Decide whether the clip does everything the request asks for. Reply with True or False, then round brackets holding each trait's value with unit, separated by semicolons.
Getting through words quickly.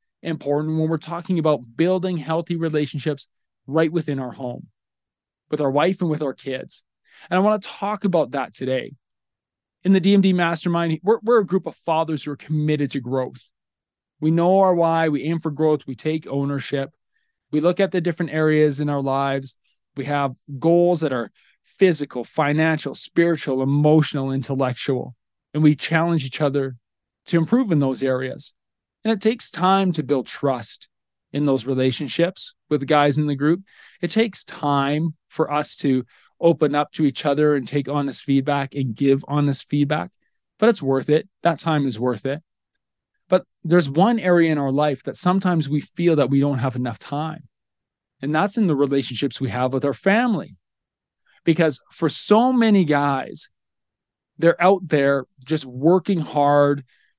False (170 wpm)